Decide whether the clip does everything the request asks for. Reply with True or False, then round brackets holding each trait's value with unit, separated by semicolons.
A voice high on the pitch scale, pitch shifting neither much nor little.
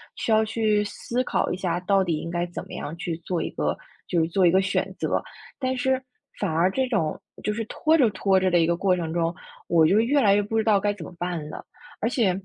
True (195 Hz; 4.3 semitones)